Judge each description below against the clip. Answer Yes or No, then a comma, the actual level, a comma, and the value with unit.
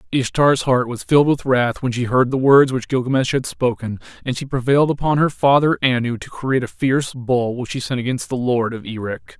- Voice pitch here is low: Yes, low, 130 Hz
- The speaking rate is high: Yes, fast, 225 wpm